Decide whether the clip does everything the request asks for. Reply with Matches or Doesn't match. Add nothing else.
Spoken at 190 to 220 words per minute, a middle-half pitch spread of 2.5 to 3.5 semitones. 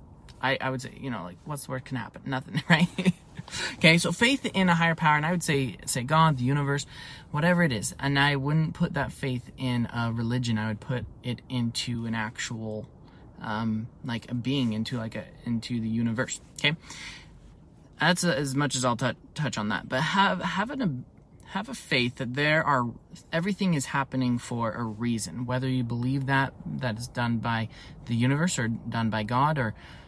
Doesn't match